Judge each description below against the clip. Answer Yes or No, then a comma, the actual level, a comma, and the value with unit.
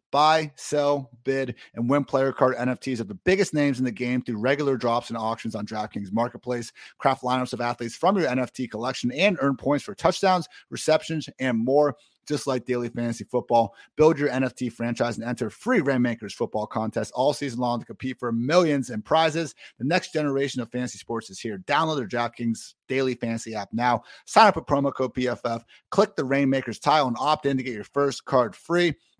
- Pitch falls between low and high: No, low, 130 Hz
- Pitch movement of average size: Yes, average, 3.2 semitones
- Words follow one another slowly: No, average, 200 wpm